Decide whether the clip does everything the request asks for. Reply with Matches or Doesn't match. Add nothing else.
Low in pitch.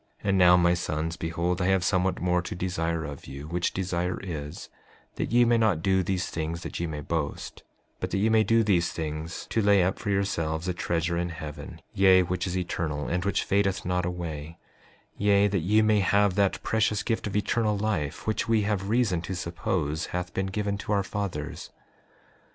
Matches